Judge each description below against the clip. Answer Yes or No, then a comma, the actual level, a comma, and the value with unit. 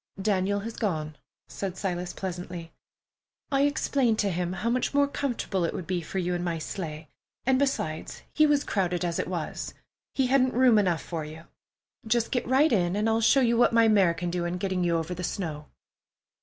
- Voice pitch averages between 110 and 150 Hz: No, high, 190 Hz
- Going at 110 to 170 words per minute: No, average, 200 wpm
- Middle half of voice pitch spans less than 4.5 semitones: No, average, 5.2 semitones